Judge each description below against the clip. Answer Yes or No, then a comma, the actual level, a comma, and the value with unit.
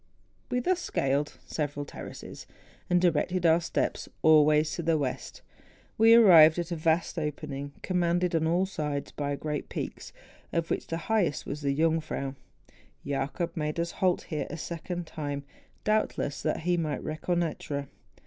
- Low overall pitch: No, medium, 160 Hz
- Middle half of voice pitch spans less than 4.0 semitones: Yes, average, 2.9 semitones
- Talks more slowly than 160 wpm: Yes, average, 150 wpm